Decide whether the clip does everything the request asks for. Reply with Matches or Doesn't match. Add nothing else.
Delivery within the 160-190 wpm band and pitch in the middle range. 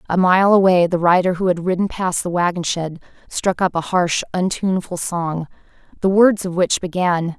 Matches